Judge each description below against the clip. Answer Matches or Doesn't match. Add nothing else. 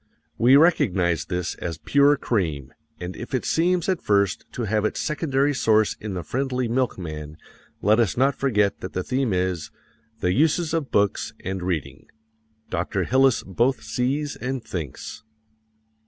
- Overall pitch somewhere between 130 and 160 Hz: Doesn't match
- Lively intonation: Matches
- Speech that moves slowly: Doesn't match